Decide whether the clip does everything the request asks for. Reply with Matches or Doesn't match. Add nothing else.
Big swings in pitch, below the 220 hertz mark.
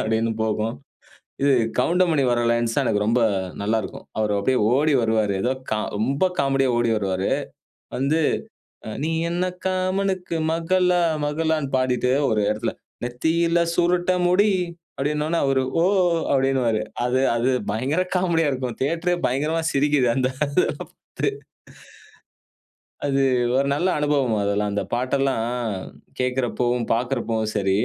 Matches